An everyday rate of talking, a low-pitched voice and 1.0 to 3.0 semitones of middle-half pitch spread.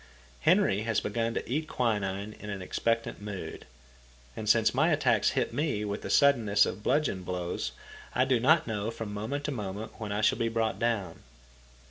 Yes: average, 180 wpm; low, 110 Hz; average, 2.7 semitones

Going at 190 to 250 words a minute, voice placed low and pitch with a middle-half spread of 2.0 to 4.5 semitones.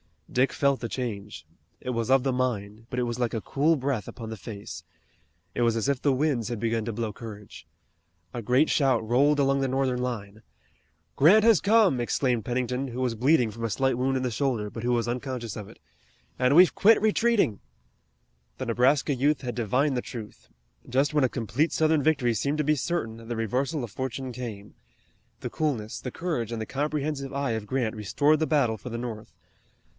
Yes: average, 200 wpm; low, 125 Hz; average, 3.5 semitones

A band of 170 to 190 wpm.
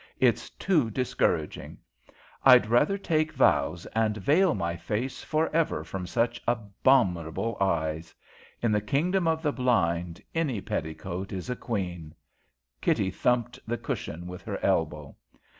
No: slow, 135 wpm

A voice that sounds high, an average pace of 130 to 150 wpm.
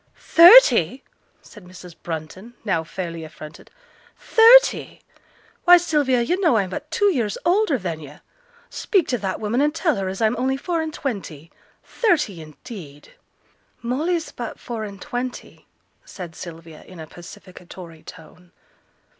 Yes: high, 215 Hz; average, 140 wpm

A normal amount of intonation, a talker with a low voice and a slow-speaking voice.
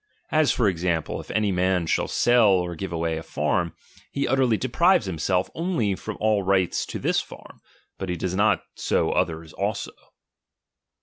No: average, 4.3 semitones; very low, 95 Hz; average, 175 wpm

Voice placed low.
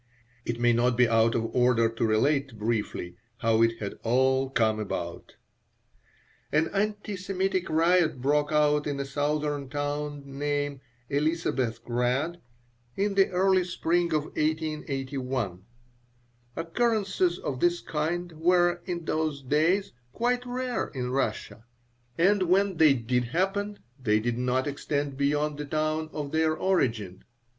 No: medium, 145 Hz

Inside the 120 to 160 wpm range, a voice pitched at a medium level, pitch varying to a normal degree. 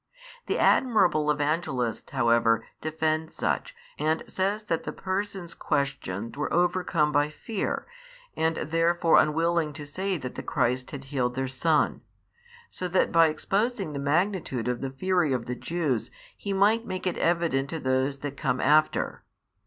Yes: average, 155 wpm; medium, 155 Hz; average, 4.7 semitones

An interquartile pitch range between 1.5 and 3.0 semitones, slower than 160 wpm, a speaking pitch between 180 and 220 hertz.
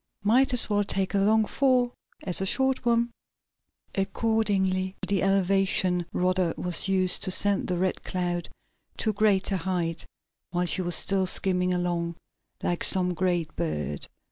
Yes: narrow, 2.4 semitones; average, 150 wpm; high, 190 Hz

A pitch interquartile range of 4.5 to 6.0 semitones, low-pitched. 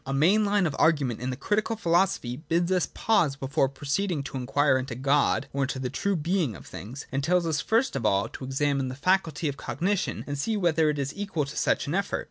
No: average, 5.0 semitones; medium, 150 Hz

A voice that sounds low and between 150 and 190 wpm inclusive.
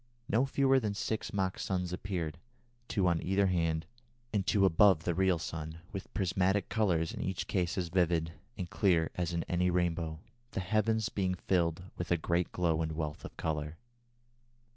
Yes: very low, 90 Hz; average, 175 wpm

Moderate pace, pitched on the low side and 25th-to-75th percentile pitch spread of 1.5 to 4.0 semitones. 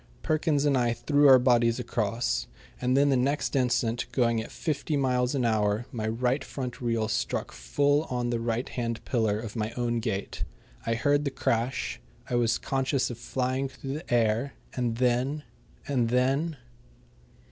Yes: average, 170 wpm; low, 125 Hz; average, 2.7 semitones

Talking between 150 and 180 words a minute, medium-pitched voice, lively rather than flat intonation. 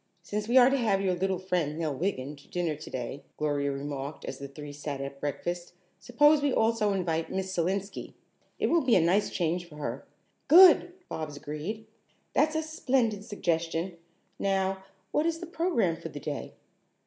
Yes: average, 175 wpm; medium, 180 Hz; wide, 6.7 semitones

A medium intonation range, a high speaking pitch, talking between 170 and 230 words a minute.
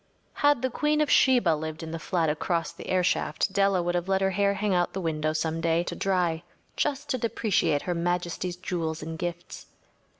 No: average, 3.3 semitones; medium, 175 Hz; average, 200 wpm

